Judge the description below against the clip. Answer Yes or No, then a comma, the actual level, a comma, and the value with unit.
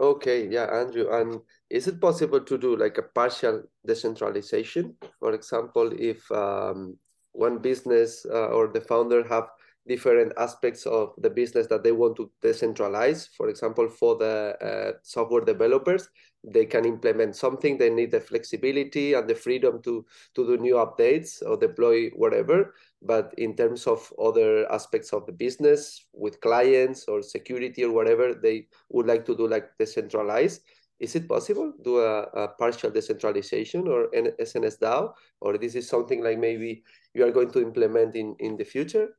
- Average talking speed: Yes, average, 165 wpm